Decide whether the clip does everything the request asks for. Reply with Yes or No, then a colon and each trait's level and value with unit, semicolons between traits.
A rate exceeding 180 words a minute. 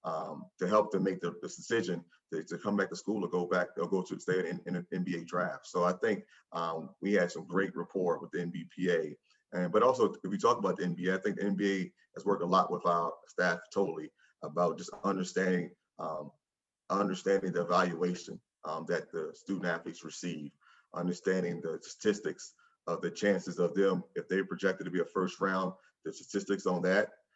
Yes: fast, 205 wpm